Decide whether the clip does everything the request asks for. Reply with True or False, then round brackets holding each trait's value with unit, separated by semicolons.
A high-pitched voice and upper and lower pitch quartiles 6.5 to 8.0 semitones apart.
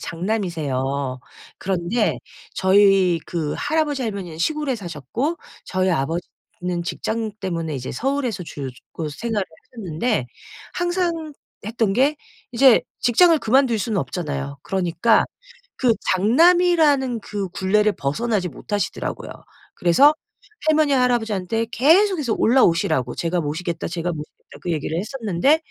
True (205 Hz; 7.2 semitones)